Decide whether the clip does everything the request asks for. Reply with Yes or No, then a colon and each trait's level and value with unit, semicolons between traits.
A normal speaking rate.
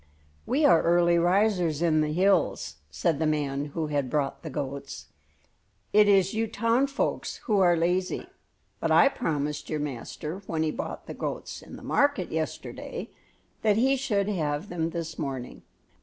Yes: average, 165 wpm